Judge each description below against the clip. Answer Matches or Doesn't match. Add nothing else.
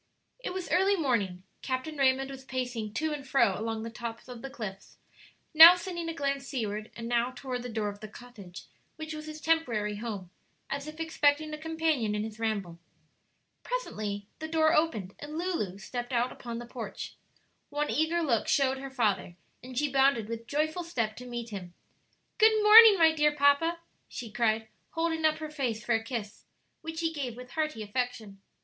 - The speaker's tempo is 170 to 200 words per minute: Matches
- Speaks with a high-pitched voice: Matches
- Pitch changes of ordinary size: Doesn't match